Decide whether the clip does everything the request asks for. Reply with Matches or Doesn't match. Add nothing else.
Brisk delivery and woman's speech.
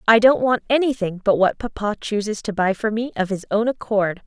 Matches